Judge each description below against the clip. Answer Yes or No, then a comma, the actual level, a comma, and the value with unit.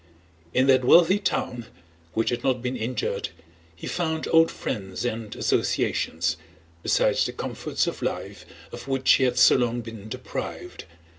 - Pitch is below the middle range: Yes, low, 125 Hz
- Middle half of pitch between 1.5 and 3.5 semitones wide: Yes, average, 2.9 semitones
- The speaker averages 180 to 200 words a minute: No, average, 150 wpm